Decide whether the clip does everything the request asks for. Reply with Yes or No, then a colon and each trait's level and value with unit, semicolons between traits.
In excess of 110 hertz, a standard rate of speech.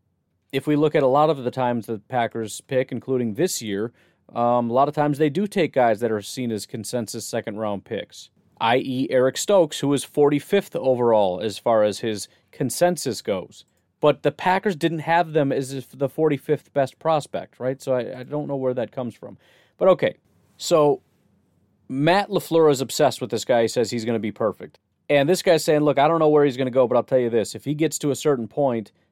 No: low, 135 Hz; fast, 225 wpm